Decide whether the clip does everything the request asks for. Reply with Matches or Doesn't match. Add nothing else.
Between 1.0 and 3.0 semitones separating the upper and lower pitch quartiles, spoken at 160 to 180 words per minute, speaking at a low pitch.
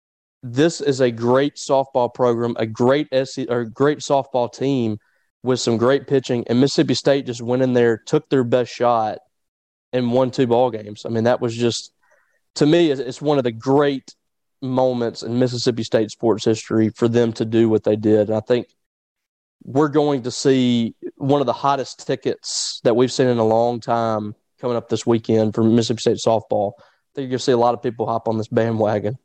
Doesn't match